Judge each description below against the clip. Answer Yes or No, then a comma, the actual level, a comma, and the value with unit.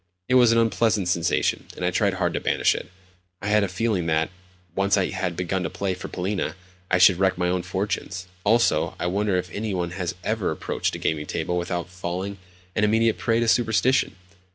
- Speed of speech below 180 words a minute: No, fast, 205 wpm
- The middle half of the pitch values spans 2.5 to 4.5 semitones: Yes, average, 3.1 semitones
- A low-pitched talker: Yes, very low, 95 Hz